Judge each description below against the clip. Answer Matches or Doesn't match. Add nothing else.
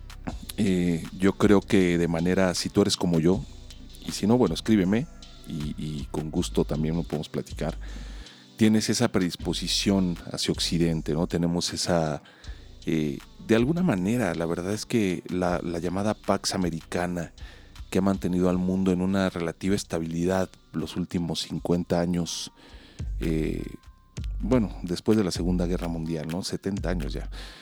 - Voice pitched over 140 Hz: Doesn't match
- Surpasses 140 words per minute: Matches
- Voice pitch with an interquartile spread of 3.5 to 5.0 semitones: Doesn't match